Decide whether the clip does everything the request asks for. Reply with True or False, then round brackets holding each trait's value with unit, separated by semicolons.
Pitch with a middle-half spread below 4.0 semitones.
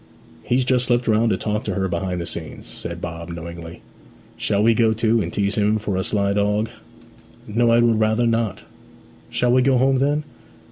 True (3.5 semitones)